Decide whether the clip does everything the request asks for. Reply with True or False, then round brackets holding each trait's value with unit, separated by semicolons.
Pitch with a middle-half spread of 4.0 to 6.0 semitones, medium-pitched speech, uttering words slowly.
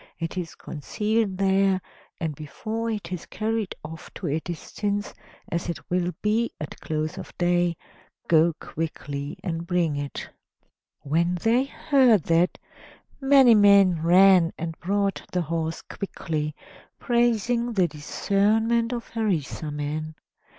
True (4.9 semitones; 180 Hz; 125 wpm)